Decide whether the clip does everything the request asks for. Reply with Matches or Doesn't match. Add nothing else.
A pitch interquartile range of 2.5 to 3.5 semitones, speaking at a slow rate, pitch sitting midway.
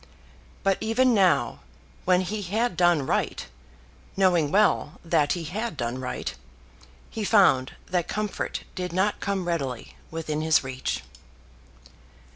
Doesn't match